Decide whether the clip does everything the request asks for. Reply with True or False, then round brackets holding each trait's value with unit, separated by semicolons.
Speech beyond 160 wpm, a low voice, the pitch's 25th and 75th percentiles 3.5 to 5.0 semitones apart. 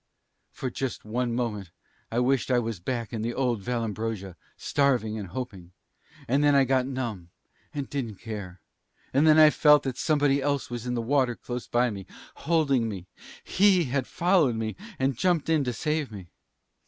True (180 wpm; 125 Hz; 3.9 semitones)